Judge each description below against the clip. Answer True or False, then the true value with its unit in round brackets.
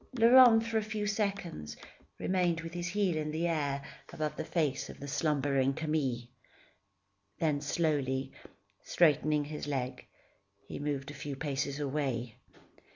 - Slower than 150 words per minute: True (140 wpm)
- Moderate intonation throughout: True (3.8 semitones)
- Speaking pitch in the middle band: True (150 Hz)